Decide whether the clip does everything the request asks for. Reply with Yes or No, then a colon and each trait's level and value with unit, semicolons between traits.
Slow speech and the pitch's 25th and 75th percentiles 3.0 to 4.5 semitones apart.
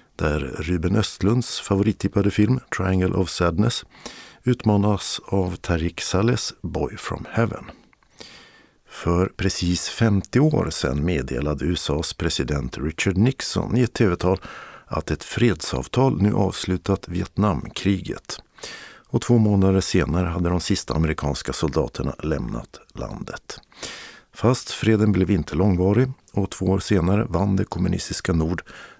Yes: slow, 120 wpm; average, 3.3 semitones